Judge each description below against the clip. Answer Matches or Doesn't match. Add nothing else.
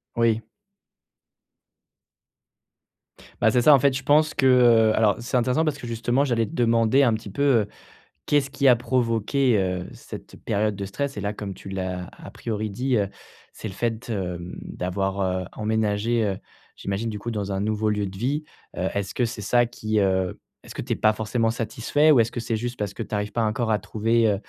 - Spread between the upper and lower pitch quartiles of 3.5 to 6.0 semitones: Doesn't match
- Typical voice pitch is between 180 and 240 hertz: Doesn't match